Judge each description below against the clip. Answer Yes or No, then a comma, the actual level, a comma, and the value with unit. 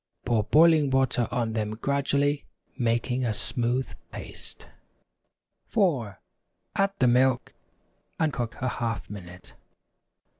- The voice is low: Yes, low, 125 Hz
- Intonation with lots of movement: No, average, 3.6 semitones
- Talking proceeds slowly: Yes, slow, 110 wpm